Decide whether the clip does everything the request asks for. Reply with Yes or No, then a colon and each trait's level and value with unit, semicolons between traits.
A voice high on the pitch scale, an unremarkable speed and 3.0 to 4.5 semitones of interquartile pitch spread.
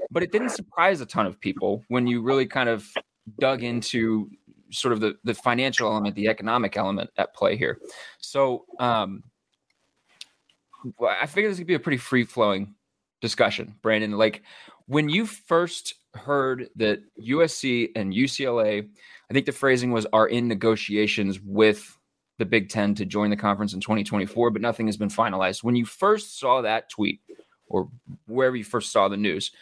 No: low, 115 Hz; average, 170 wpm; average, 4.2 semitones